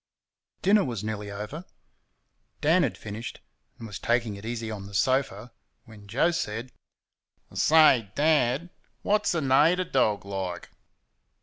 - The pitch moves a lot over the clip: Yes, wide, 6.5 semitones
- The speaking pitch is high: No, low, 120 Hz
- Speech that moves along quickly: No, slow, 135 wpm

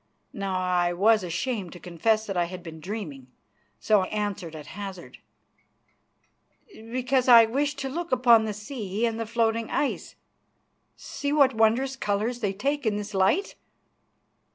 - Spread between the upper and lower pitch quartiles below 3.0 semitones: No, average, 4.7 semitones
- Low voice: No, high, 220 Hz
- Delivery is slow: No, average, 155 wpm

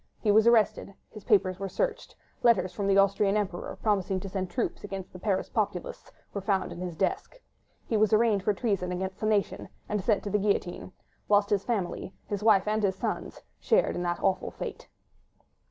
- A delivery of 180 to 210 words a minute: Yes, average, 190 wpm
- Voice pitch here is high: Yes, high, 200 Hz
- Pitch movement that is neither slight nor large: No, narrow, 2.0 semitones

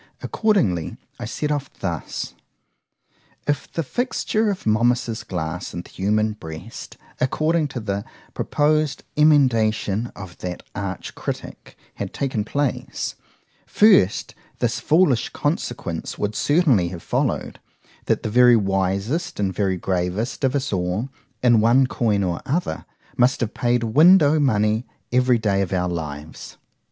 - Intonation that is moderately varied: No, wide, 6.7 semitones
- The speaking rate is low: Yes, slow, 130 wpm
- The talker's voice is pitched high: No, low, 115 Hz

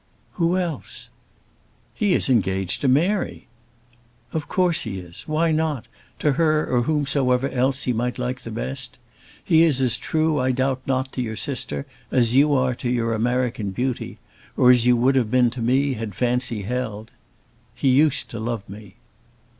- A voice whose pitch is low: Yes, low, 125 Hz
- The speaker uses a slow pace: No, average, 170 wpm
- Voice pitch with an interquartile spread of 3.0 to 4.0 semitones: Yes, average, 3.4 semitones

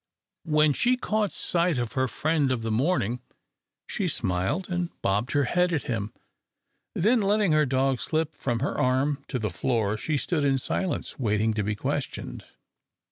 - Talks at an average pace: Yes, average, 170 wpm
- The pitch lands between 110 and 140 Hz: Yes, low, 135 Hz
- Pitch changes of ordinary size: No, wide, 6.5 semitones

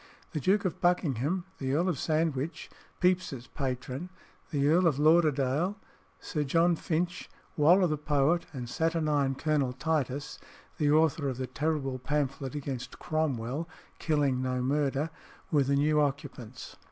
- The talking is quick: No, average, 140 wpm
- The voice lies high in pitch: No, medium, 150 Hz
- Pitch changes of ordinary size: Yes, average, 3.2 semitones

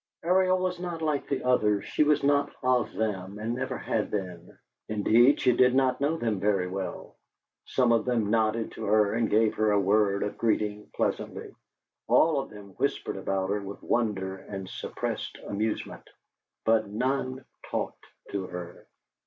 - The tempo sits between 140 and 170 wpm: Yes, average, 165 wpm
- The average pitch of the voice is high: No, low, 110 Hz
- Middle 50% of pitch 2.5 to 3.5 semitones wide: No, average, 4.2 semitones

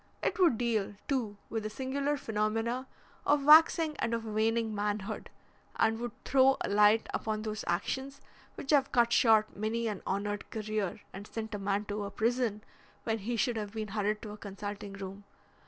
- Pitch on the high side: Yes, high, 220 Hz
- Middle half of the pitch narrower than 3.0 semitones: Yes, narrow, 2.5 semitones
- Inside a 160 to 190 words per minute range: Yes, average, 180 wpm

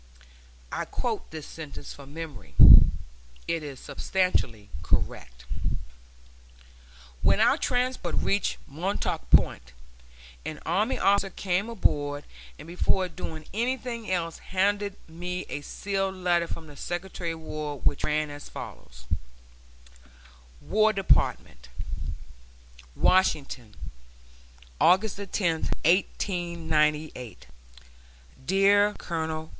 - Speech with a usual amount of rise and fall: Yes, average, 4.6 semitones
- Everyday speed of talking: No, slow, 100 wpm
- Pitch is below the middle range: No, medium, 170 Hz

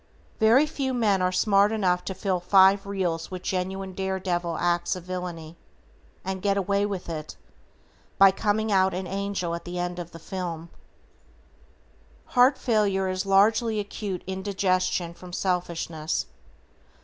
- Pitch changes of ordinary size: No, narrow, 2.1 semitones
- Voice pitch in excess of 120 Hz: Yes, high, 190 Hz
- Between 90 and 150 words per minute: Yes, average, 145 wpm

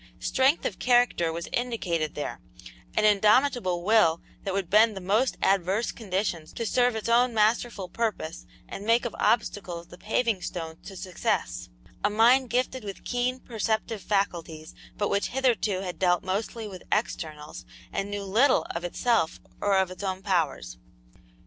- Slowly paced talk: No, average, 155 wpm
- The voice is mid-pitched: No, high, 205 Hz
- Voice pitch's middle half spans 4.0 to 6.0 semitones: Yes, average, 4.5 semitones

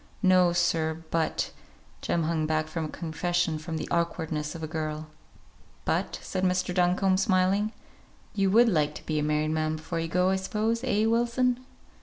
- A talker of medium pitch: Yes, medium, 170 Hz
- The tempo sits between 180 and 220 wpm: Yes, average, 185 wpm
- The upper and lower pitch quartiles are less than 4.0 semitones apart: Yes, average, 3.2 semitones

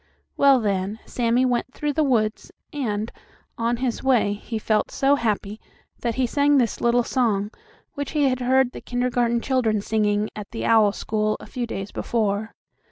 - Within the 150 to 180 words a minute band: Yes, average, 170 wpm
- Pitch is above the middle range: Yes, high, 235 Hz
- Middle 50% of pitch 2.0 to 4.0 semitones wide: Yes, average, 3.3 semitones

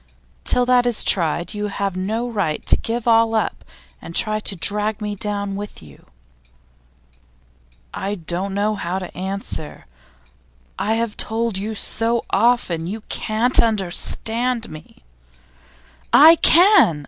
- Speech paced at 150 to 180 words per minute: No, slow, 135 wpm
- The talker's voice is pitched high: Yes, high, 210 Hz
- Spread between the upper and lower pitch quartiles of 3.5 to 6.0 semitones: No, average, 3.1 semitones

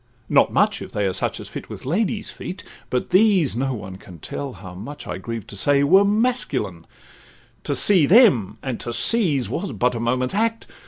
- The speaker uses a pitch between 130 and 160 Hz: Yes, medium, 140 Hz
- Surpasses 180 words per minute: Yes, average, 200 wpm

